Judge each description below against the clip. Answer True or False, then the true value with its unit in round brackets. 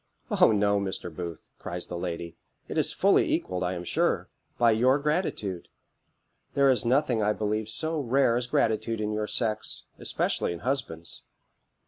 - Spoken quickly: False (160 wpm)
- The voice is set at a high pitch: False (110 Hz)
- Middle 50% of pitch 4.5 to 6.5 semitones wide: True (5.4 semitones)